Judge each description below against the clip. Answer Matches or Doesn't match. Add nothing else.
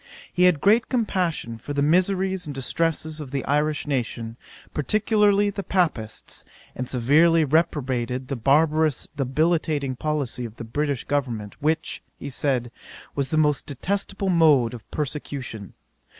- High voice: Doesn't match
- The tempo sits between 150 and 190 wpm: Doesn't match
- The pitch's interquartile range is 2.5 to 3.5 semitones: Doesn't match